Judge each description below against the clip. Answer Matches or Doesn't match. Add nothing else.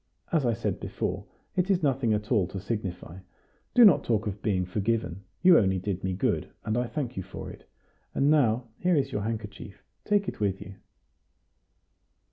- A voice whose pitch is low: Matches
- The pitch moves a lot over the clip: Matches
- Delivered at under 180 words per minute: Doesn't match